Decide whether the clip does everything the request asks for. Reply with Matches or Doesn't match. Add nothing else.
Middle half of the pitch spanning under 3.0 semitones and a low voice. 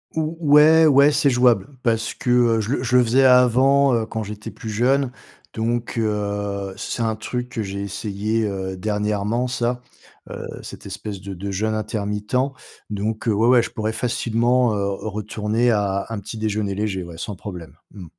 Doesn't match